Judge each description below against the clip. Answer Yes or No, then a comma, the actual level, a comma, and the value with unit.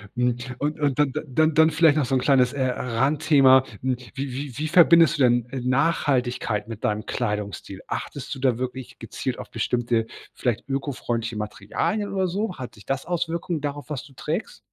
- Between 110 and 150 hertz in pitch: Yes, low, 135 Hz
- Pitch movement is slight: No, average, 3.8 semitones